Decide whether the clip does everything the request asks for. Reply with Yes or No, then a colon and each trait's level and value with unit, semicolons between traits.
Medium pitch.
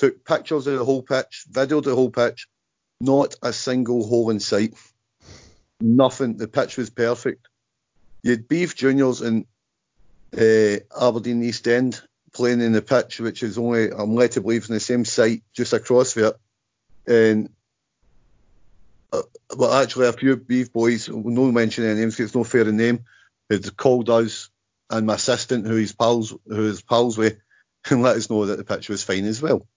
No: low, 115 Hz